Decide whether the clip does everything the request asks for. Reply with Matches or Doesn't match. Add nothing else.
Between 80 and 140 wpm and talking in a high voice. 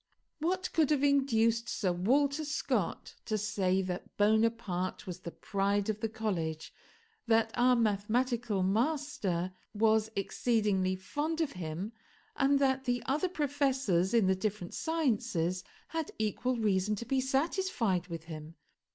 Matches